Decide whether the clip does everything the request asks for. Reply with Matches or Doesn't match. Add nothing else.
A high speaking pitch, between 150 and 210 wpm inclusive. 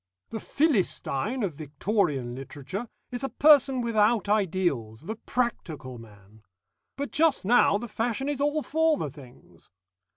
Doesn't match